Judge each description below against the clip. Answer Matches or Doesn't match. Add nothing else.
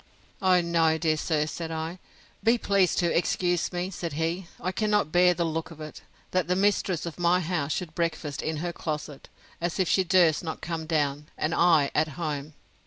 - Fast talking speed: Doesn't match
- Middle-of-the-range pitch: Matches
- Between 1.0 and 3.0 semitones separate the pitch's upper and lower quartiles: Matches